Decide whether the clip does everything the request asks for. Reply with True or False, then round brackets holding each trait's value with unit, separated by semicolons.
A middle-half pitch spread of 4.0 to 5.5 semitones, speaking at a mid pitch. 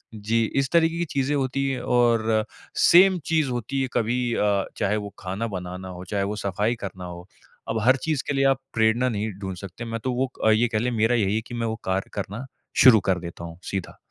False (4.6 semitones; 115 Hz)